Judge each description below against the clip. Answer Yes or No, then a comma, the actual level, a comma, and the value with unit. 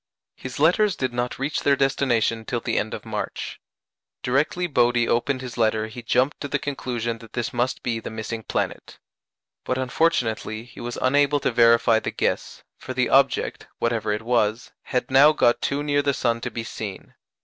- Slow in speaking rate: No, average, 185 wpm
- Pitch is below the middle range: Yes, low, 120 Hz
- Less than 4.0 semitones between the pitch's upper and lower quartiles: Yes, average, 3.1 semitones